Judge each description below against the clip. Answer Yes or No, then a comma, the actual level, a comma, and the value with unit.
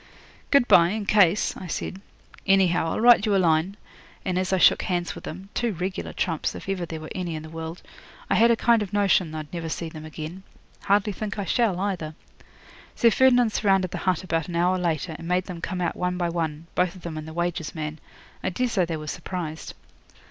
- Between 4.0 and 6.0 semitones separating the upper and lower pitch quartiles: No, average, 3.1 semitones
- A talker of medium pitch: Yes, medium, 180 Hz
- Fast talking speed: Yes, fast, 220 wpm